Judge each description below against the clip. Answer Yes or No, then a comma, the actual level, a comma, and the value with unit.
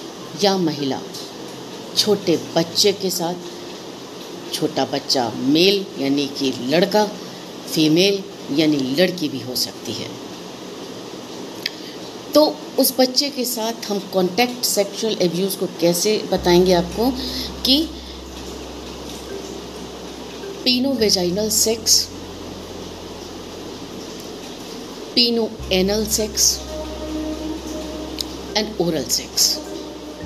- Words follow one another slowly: Yes, slow, 85 wpm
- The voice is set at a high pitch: Yes, high, 200 Hz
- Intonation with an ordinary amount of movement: No, wide, 5.7 semitones